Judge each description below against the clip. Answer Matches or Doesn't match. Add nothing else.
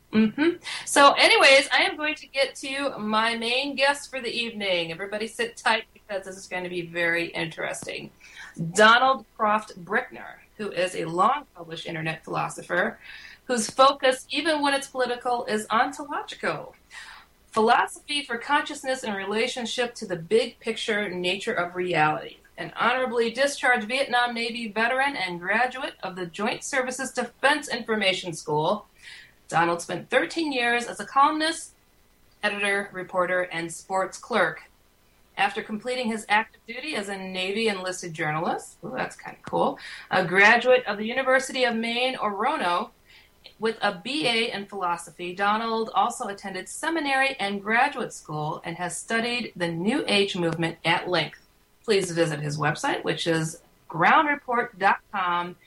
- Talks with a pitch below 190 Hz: Doesn't match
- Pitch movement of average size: Doesn't match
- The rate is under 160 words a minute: Matches